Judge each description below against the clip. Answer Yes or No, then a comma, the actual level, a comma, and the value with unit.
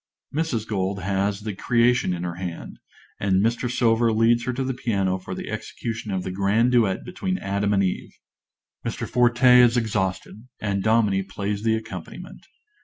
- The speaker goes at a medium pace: Yes, average, 170 wpm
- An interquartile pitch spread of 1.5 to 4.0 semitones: Yes, average, 3.5 semitones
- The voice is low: Yes, low, 110 Hz